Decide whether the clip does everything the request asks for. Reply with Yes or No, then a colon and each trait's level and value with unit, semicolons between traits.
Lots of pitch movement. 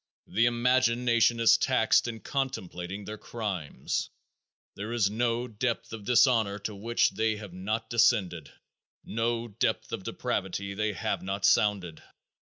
No: average, 2.9 semitones